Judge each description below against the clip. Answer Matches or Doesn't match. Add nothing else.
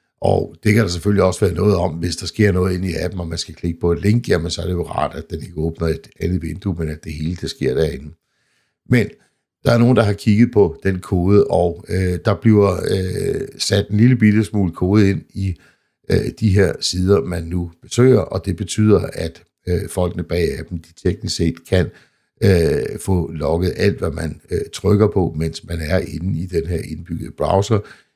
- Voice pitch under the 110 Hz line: Matches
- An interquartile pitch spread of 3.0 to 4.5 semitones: Matches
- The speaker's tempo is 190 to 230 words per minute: Matches